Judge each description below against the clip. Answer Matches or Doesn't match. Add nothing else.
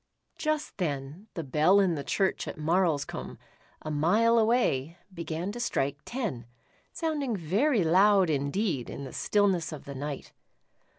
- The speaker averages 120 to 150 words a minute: Matches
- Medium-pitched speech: Matches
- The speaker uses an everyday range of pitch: Doesn't match